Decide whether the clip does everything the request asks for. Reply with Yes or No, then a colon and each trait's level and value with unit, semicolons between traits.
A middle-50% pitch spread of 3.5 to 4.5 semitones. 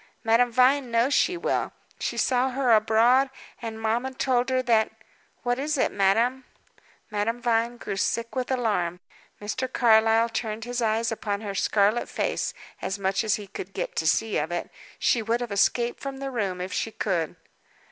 No: average, 3.0 semitones